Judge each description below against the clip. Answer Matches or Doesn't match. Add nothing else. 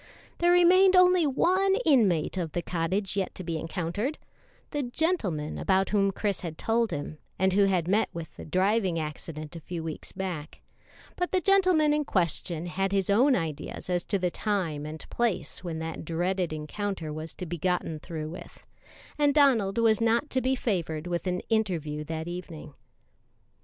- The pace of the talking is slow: Doesn't match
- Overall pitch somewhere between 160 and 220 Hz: Matches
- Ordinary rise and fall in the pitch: Doesn't match